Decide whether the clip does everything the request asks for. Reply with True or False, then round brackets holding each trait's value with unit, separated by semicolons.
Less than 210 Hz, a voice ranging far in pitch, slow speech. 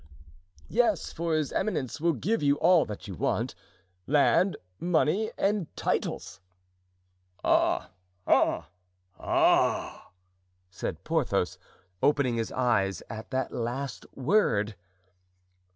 True (140 Hz; 7.4 semitones; 100 wpm)